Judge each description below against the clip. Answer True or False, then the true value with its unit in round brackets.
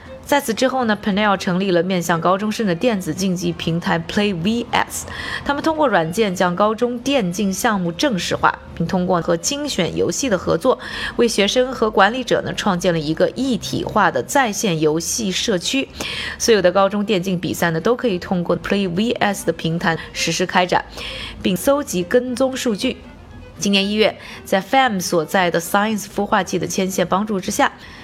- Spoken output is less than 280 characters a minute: False (310 characters per minute)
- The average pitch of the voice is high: True (200 Hz)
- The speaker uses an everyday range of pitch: True (4.7 semitones)